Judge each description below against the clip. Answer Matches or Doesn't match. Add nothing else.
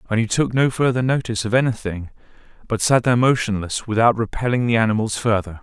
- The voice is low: Matches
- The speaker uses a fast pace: Doesn't match